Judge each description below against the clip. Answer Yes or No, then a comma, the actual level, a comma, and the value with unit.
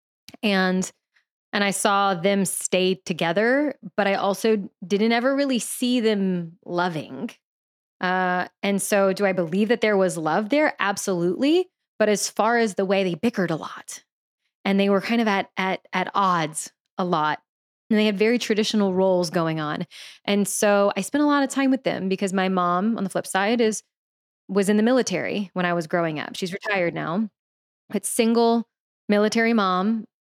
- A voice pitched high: Yes, high, 200 Hz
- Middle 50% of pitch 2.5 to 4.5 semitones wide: Yes, average, 3.1 semitones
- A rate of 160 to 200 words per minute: Yes, average, 180 wpm